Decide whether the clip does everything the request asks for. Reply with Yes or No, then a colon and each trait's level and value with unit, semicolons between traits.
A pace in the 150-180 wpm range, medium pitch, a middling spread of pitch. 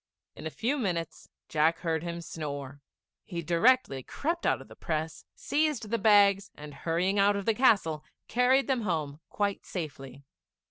No: average, 160 wpm; medium, 175 Hz; wide, 6.0 semitones